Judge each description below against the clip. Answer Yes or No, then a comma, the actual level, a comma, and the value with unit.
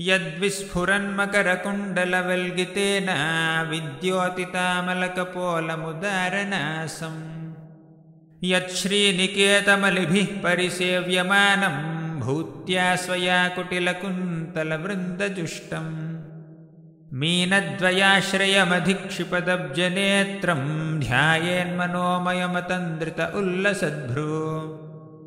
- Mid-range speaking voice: Yes, medium, 180 Hz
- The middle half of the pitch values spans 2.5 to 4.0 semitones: Yes, average, 2.8 semitones